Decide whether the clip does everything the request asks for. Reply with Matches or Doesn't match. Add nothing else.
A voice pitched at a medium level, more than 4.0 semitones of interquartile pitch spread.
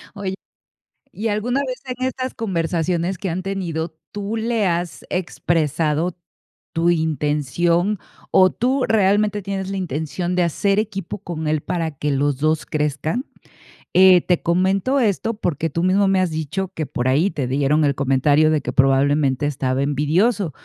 Matches